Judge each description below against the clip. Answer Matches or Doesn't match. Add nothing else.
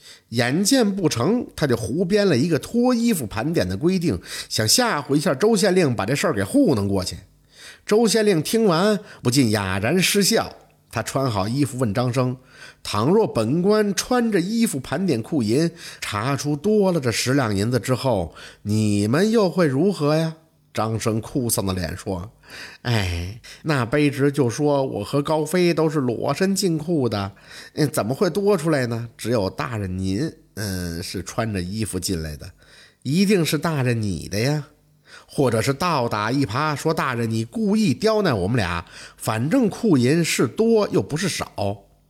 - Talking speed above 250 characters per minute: Doesn't match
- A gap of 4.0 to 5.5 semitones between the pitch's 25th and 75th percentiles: Doesn't match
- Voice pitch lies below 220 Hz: Matches